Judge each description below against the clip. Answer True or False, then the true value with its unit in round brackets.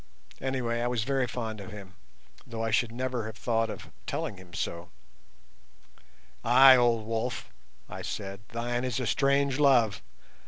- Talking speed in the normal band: True (155 wpm)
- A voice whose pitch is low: True (120 Hz)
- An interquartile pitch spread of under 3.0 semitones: True (2.6 semitones)